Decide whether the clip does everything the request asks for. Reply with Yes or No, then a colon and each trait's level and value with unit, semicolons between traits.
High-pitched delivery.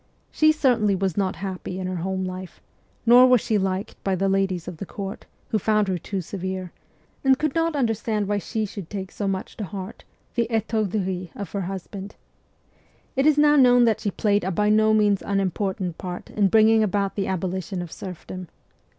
Yes: high, 200 Hz